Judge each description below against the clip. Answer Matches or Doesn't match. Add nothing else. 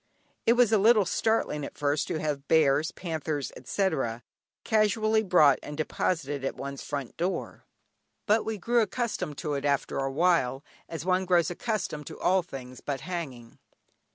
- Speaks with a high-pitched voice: Doesn't match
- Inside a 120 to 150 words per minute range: Doesn't match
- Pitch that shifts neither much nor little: Doesn't match